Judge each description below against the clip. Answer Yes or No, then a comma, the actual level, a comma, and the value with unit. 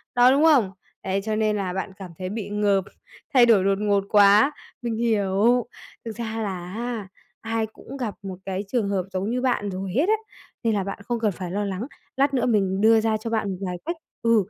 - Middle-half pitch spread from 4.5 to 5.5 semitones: No, average, 3.1 semitones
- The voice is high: Yes, high, 210 Hz